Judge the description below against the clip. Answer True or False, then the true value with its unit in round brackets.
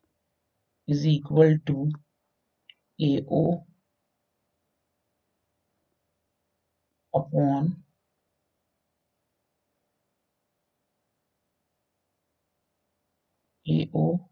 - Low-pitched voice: True (100 Hz)